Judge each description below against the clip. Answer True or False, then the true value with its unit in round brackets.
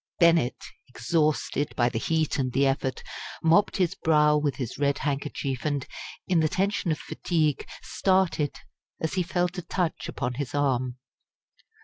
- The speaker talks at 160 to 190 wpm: False (150 wpm)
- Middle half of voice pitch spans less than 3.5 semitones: False (3.8 semitones)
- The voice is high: False (150 Hz)